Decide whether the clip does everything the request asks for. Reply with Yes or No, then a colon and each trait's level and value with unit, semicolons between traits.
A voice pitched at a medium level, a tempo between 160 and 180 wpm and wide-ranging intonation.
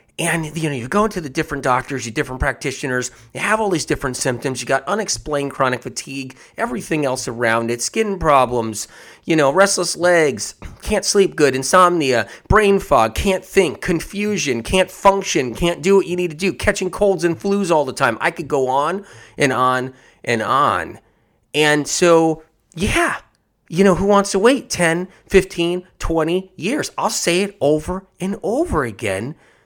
Yes: medium, 165 Hz; average, 175 wpm; wide, 6.0 semitones